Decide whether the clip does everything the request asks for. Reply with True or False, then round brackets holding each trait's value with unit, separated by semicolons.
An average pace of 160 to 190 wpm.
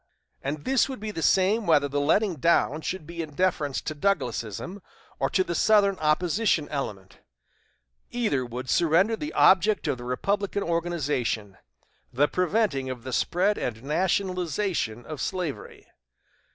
False (145 wpm)